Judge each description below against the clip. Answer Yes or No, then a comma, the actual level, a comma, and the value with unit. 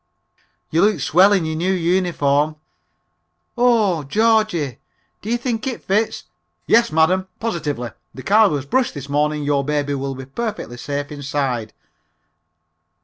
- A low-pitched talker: No, medium, 160 Hz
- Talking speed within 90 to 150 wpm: Yes, average, 140 wpm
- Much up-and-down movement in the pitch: Yes, wide, 6.9 semitones